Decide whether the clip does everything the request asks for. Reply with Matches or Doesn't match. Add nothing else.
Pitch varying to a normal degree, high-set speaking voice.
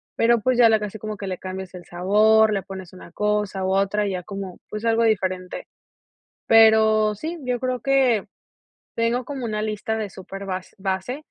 Matches